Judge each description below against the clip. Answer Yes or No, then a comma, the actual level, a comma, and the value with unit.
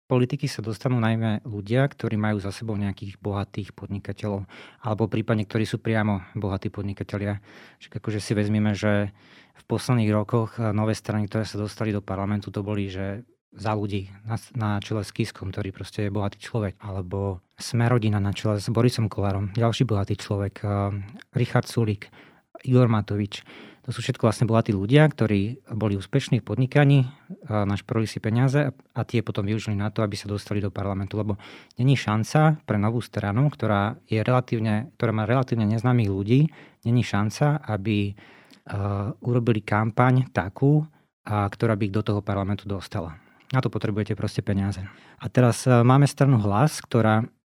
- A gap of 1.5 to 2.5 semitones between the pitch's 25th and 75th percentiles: No, average, 2.9 semitones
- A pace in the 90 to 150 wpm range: No, average, 160 wpm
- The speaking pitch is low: Yes, low, 110 Hz